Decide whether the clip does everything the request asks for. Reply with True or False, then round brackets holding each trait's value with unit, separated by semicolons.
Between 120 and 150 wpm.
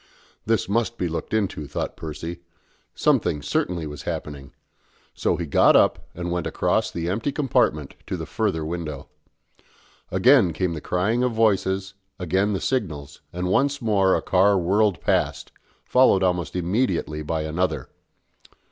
True (145 wpm)